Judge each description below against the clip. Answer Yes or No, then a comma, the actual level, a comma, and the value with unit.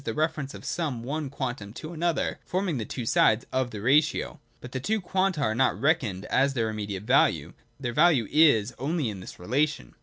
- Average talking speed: Yes, average, 195 wpm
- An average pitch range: No, wide, 5.9 semitones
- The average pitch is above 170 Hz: No, low, 130 Hz